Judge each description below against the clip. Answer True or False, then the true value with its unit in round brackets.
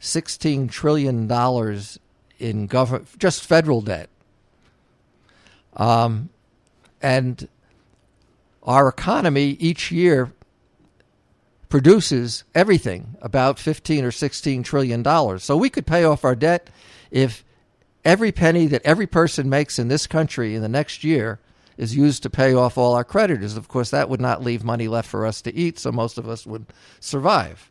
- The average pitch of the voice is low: True (130 Hz)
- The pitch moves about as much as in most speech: True (4.8 semitones)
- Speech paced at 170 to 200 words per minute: False (150 wpm)